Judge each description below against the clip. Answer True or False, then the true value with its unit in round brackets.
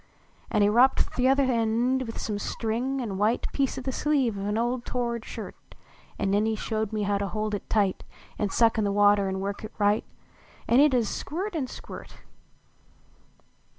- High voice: True (225 Hz)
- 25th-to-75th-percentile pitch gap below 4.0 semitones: True (3.6 semitones)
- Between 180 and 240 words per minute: True (195 wpm)